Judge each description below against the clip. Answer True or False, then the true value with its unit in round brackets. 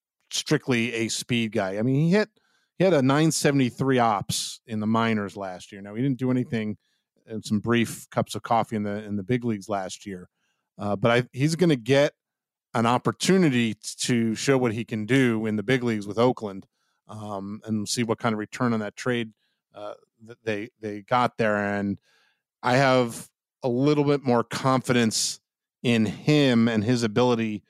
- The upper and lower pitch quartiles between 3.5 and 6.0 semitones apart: False (3.1 semitones)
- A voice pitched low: True (115 Hz)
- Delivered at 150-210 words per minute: True (190 wpm)